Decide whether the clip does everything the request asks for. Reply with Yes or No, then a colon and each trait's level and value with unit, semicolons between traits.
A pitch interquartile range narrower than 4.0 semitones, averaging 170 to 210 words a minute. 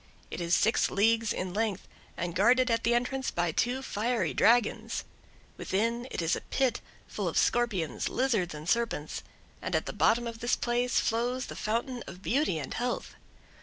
No: average, 4.6 semitones; average, 175 wpm